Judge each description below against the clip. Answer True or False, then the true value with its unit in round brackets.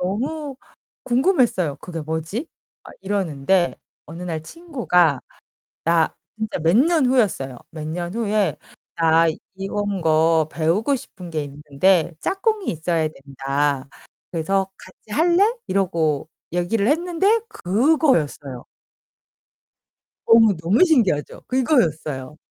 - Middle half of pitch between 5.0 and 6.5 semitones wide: False (7.4 semitones)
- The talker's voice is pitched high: False (180 Hz)